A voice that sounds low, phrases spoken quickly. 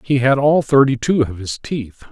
Yes: low, 130 Hz; fast, 225 wpm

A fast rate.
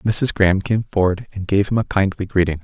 Yes: fast, 230 wpm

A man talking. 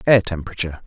Yes: male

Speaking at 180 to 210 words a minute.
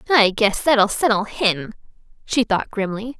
No: average, 150 wpm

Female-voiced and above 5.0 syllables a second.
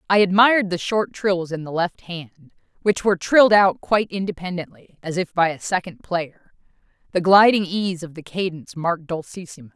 Yes: female; 5.4 syllables/s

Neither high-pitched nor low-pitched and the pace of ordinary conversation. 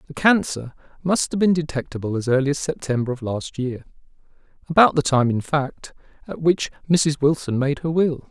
Yes: medium, 145 Hz; average, 180 wpm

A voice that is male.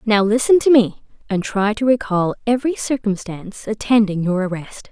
No: female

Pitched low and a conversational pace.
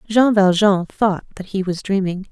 No: high, 195 Hz; average, 180 wpm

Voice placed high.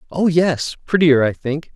No: medium, 155 Hz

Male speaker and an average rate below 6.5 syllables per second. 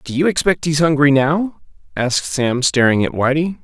Yes: male; 5.0 syllables/s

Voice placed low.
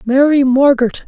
No: very high, 265 Hz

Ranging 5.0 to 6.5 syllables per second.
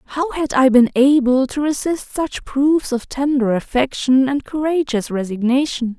No: 4.2 syllables/s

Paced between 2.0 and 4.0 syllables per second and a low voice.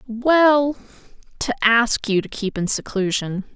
No: 3.8 syllables/s; high, 230 Hz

